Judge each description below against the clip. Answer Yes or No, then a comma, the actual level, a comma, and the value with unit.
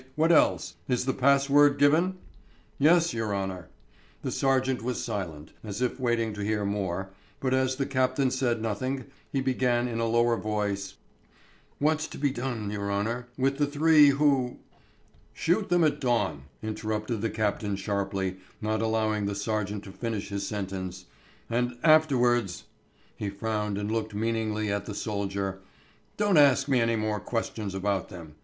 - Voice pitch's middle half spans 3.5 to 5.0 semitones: Yes, average, 4.5 semitones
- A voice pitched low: Yes, low, 115 Hz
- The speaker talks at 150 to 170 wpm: Yes, average, 160 wpm